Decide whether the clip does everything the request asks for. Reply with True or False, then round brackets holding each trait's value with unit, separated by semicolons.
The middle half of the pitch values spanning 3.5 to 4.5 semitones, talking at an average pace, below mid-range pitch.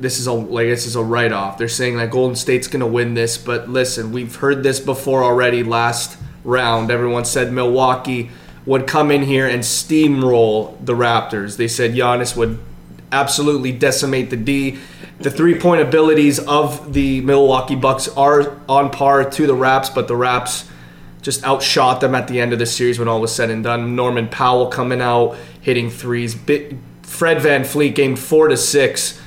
False (2.7 semitones; 180 wpm; 125 Hz)